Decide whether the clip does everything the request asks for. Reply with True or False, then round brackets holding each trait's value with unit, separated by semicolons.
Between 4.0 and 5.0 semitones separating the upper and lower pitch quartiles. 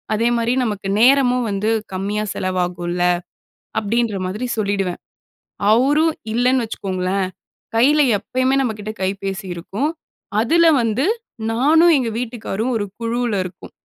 True (4.3 semitones)